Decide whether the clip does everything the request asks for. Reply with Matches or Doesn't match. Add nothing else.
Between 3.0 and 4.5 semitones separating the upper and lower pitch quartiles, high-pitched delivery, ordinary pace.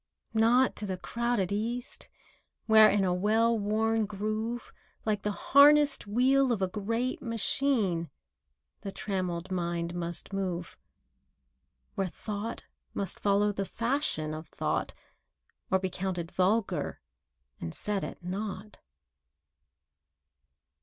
Doesn't match